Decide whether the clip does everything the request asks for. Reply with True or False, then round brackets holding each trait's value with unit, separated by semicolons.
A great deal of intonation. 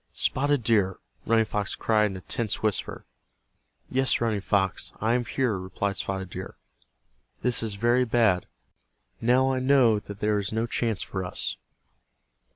False (3.4 semitones)